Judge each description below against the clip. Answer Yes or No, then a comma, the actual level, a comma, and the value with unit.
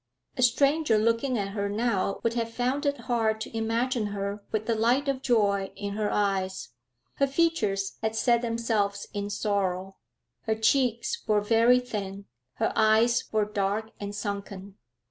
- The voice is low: No, high, 220 Hz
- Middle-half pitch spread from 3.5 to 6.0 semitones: No, average, 2.8 semitones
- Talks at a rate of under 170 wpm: Yes, average, 160 wpm